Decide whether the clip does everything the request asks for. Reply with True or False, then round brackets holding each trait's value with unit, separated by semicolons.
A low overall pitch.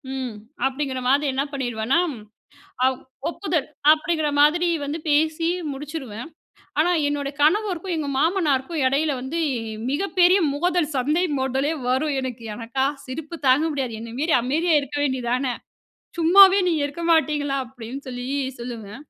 False (290 Hz)